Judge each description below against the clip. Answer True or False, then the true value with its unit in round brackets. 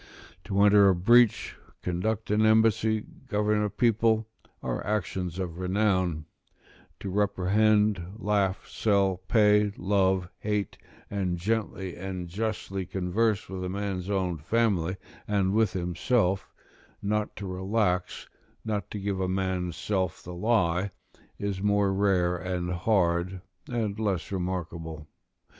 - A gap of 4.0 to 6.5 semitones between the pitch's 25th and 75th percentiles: False (2.6 semitones)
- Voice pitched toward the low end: True (95 Hz)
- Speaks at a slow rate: True (125 wpm)